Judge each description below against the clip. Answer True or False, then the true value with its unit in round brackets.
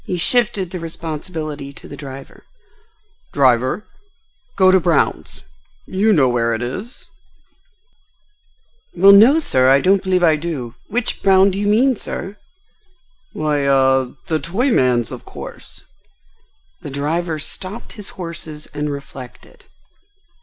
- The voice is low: False (160 Hz)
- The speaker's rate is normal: False (125 wpm)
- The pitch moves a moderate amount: False (5.8 semitones)